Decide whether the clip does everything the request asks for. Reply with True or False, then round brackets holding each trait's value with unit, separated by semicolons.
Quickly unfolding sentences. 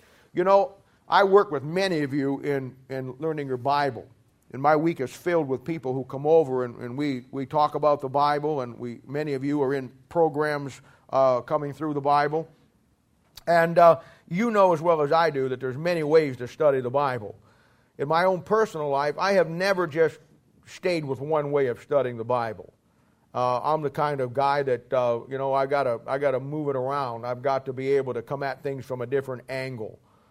True (215 wpm)